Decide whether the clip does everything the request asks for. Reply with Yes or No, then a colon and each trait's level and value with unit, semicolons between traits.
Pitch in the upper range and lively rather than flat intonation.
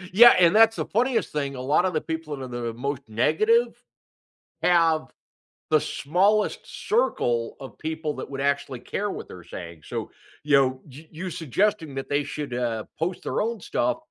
No: medium, 155 Hz; wide, 6.0 semitones